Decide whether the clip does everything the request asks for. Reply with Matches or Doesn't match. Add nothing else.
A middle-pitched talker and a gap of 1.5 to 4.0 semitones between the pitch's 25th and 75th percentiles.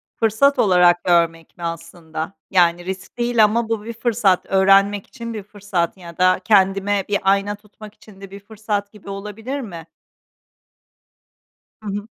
Doesn't match